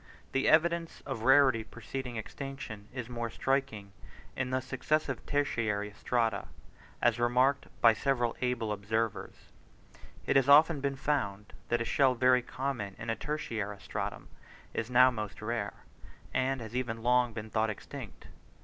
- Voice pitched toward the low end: Yes, low, 120 Hz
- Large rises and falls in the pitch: No, average, 3.4 semitones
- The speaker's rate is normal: Yes, average, 145 wpm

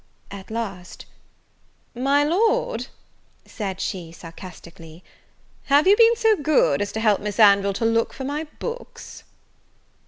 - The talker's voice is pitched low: No, high, 225 Hz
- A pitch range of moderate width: No, wide, 8.3 semitones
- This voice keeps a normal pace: No, slow, 130 wpm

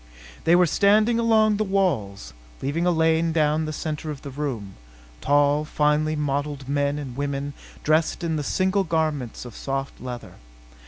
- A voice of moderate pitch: Yes, medium, 150 Hz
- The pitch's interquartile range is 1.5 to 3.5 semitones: Yes, average, 2.9 semitones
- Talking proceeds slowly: No, average, 160 wpm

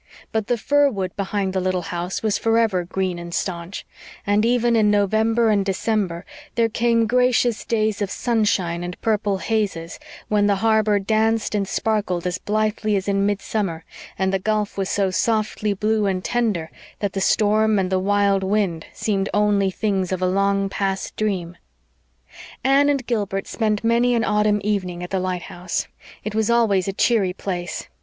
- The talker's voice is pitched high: Yes, high, 205 Hz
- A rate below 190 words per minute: Yes, average, 170 wpm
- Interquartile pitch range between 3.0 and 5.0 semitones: No, narrow, 2.5 semitones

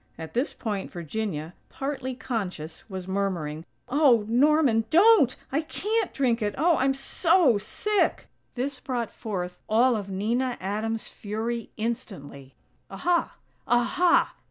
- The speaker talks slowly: Yes, slow, 125 wpm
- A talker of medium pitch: No, high, 235 Hz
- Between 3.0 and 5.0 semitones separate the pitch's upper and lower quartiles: No, wide, 5.4 semitones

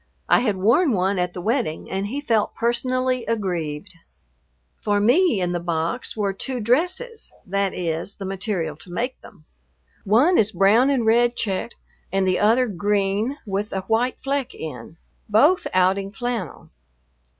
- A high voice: Yes, high, 210 Hz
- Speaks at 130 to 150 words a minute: No, average, 160 wpm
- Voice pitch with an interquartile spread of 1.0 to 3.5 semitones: No, average, 4.6 semitones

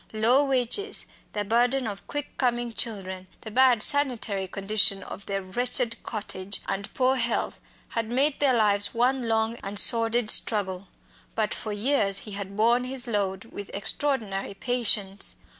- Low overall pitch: No, high, 225 Hz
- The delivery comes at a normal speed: Yes, average, 150 wpm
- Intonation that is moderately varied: Yes, average, 3.7 semitones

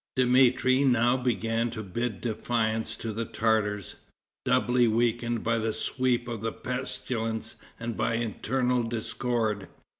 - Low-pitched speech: Yes, low, 115 Hz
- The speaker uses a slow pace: Yes, slow, 130 wpm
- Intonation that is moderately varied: No, narrow, 1.7 semitones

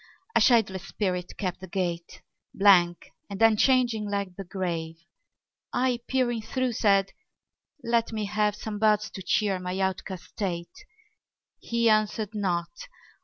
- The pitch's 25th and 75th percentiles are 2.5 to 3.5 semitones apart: Yes, average, 3.2 semitones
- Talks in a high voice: Yes, high, 200 Hz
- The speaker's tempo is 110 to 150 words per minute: Yes, slow, 135 wpm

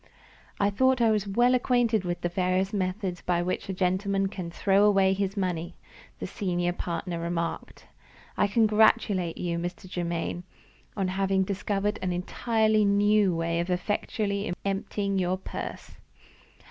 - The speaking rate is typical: Yes, average, 145 wpm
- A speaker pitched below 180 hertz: No, high, 195 Hz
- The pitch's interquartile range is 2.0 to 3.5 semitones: Yes, narrow, 2.6 semitones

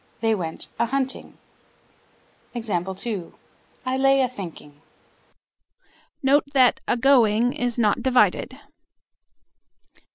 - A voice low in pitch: No, high, 240 Hz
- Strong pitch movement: No, average, 4.2 semitones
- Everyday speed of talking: No, slow, 85 wpm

